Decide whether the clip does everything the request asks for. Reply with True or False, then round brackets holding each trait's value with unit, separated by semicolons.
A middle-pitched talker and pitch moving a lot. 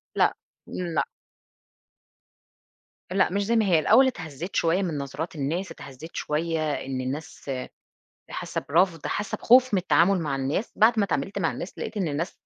False (170 Hz; 4.8 semitones)